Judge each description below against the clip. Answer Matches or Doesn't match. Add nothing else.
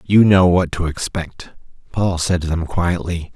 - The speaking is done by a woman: Doesn't match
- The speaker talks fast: Doesn't match